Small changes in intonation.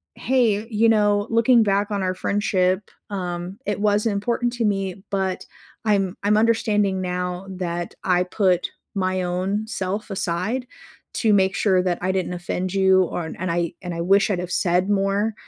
Yes: narrow, 2.3 semitones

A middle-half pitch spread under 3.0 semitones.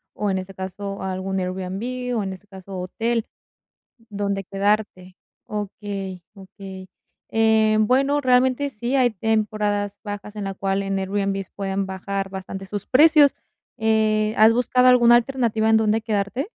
Yes: narrow, 2.6 semitones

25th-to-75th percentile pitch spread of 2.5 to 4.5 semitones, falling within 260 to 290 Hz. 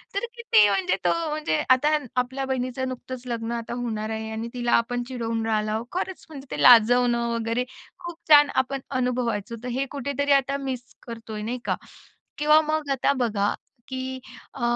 No: average, 3.1 semitones; very high, 250 Hz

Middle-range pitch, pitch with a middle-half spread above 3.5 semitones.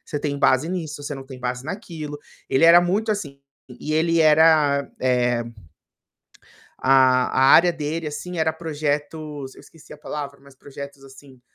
No: medium, 145 Hz; average, 2.9 semitones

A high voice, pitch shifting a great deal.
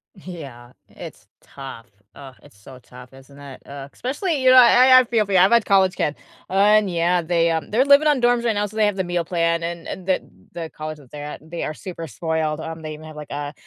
No: medium, 170 Hz; wide, 5.7 semitones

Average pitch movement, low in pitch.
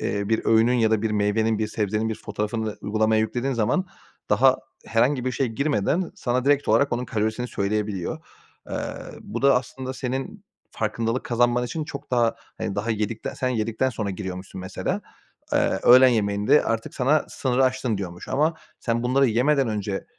Yes: average, 3.2 semitones; low, 115 Hz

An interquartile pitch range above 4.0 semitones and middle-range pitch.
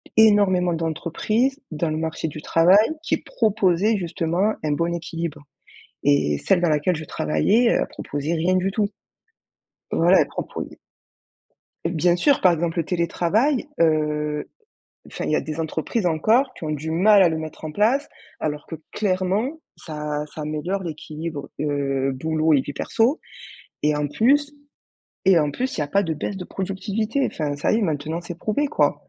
Yes: average, 4.9 semitones; medium, 170 Hz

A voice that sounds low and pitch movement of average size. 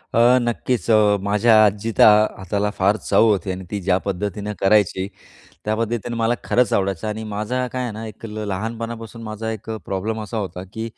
No: low, 110 Hz; narrow, 2.1 semitones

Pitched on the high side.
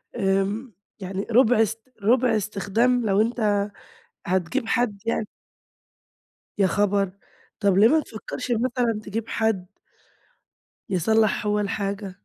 Yes: high, 215 Hz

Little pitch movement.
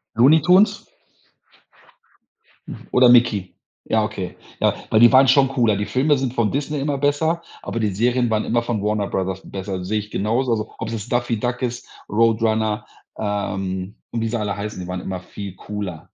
No: average, 3.5 semitones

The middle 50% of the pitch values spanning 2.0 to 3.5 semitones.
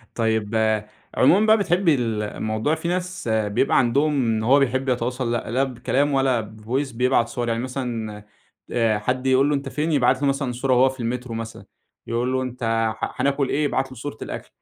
Yes: average, 3.1 semitones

